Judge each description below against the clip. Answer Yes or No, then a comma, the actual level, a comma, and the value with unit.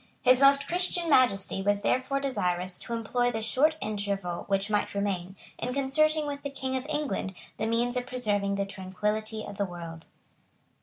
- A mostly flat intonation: No, average, 5.3 semitones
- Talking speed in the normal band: Yes, average, 170 wpm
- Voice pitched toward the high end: Yes, high, 220 Hz